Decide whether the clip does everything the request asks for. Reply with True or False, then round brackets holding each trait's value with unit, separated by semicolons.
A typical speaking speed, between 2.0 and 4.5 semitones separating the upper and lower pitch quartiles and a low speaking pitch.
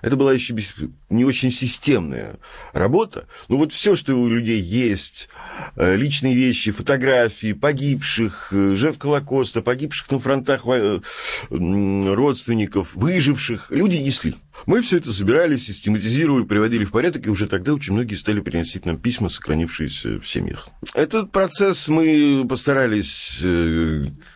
False (125 wpm; 5.6 semitones; 120 Hz)